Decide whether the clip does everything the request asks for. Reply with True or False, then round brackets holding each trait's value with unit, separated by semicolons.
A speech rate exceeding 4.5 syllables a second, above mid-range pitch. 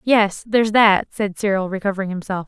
True (5.5 syllables/s; 200 Hz)